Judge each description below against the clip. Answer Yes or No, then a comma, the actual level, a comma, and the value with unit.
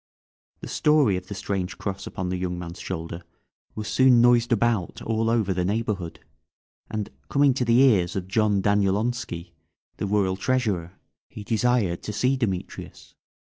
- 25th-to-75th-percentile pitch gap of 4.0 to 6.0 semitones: Yes, average, 4.3 semitones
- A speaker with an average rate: Yes, average, 155 wpm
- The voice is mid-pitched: No, low, 105 Hz